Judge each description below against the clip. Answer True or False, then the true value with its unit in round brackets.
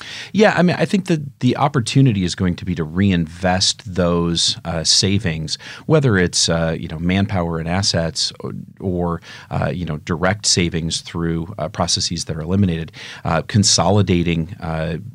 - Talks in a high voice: False (90 Hz)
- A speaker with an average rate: True (160 wpm)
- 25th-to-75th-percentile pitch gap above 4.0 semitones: True (4.8 semitones)